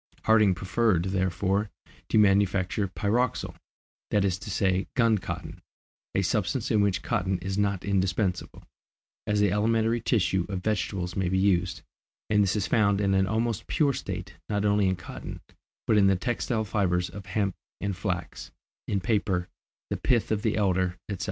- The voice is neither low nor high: No, low, 100 Hz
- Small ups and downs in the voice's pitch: Yes, narrow, 2.3 semitones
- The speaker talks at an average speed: Yes, average, 165 wpm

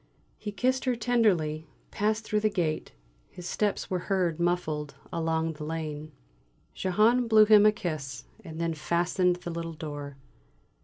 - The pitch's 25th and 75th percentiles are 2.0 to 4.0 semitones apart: No, average, 5.1 semitones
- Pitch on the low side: No, medium, 175 Hz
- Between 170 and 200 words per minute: No, average, 150 wpm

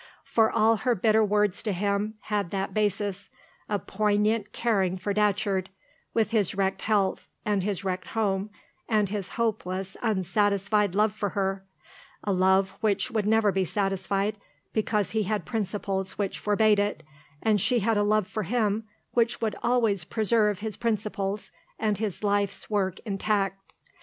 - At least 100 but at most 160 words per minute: Yes, average, 155 wpm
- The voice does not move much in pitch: Yes, narrow, 1.9 semitones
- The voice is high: Yes, high, 205 Hz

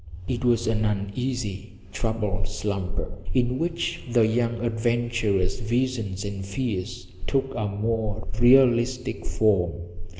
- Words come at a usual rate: No, slow, 110 wpm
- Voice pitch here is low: Yes, low, 110 Hz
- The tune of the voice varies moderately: Yes, average, 3.1 semitones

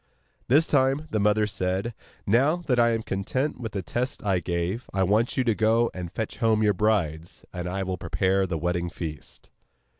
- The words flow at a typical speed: Yes, average, 190 wpm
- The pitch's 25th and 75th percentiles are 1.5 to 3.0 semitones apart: No, average, 4.4 semitones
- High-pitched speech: No, low, 105 Hz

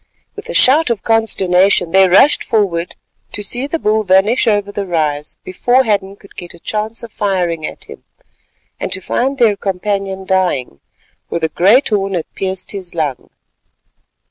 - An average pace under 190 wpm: Yes, average, 170 wpm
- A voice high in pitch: Yes, high, 195 Hz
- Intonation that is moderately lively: Yes, average, 3.5 semitones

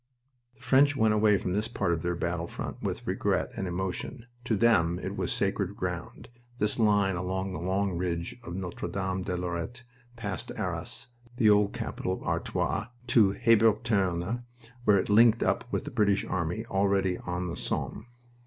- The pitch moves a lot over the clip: No, average, 3.5 semitones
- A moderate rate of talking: Yes, average, 170 wpm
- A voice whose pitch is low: Yes, low, 100 Hz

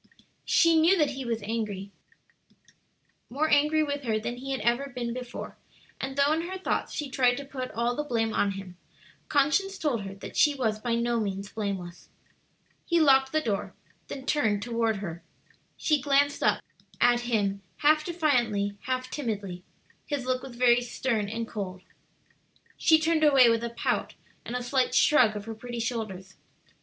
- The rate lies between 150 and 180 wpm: Yes, average, 175 wpm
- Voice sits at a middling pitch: No, high, 245 Hz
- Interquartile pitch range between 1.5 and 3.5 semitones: No, average, 4.7 semitones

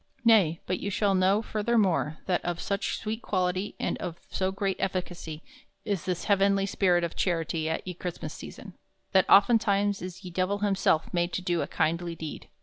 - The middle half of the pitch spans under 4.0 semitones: Yes, narrow, 2.6 semitones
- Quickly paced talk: No, average, 180 wpm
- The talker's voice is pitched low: No, medium, 185 Hz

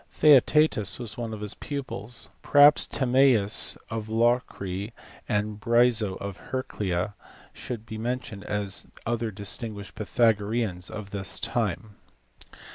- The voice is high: No, low, 110 Hz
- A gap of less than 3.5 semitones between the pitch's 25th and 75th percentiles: Yes, average, 3.0 semitones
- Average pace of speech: No, slow, 115 wpm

